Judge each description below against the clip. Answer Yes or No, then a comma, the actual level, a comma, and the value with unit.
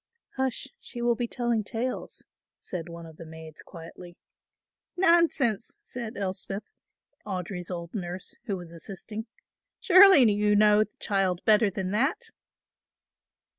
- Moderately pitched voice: No, high, 205 Hz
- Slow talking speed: Yes, slow, 130 wpm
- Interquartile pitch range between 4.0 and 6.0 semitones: Yes, average, 4.9 semitones